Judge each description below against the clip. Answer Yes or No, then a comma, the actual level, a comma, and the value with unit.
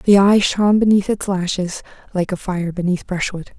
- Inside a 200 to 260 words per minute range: No, average, 185 wpm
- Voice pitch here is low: No, high, 190 Hz